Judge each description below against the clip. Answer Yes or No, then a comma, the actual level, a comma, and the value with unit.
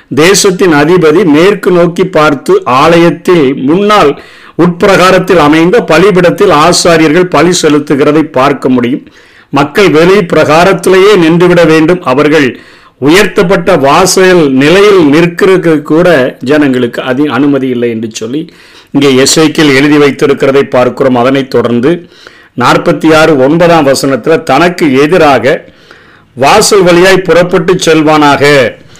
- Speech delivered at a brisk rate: No, average, 100 wpm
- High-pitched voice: No, medium, 160 Hz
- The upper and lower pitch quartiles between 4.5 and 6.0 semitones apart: No, average, 4.0 semitones